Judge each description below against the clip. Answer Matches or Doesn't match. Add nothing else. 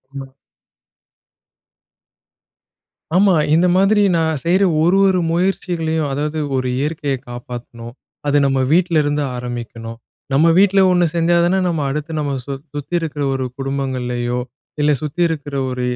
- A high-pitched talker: Doesn't match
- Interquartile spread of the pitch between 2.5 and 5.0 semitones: Matches